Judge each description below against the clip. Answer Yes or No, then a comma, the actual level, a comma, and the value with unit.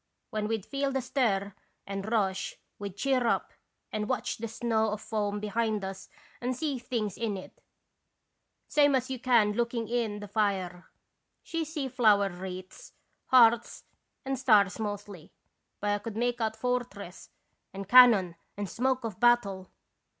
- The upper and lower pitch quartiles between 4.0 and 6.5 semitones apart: No, average, 3.5 semitones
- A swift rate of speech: No, average, 160 wpm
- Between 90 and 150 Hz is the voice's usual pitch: No, high, 220 Hz